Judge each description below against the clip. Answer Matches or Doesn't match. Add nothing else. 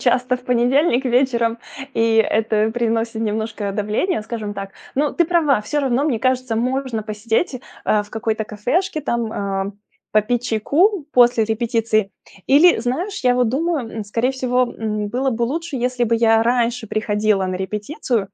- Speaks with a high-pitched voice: Matches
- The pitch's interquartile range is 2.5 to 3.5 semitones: Matches